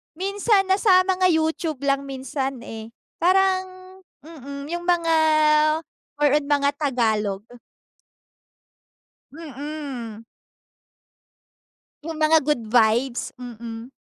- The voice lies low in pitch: No, very high, 290 Hz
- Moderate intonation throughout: No, wide, 5.8 semitones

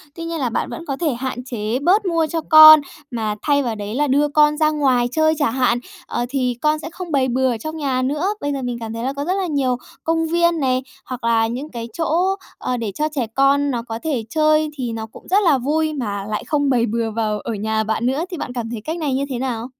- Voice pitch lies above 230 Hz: Yes, very high, 270 Hz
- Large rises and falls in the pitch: No, average, 4.6 semitones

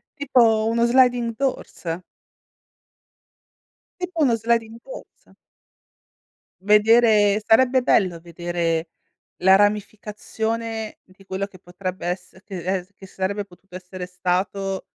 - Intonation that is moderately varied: Yes, average, 3.7 semitones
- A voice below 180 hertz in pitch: No, high, 205 Hz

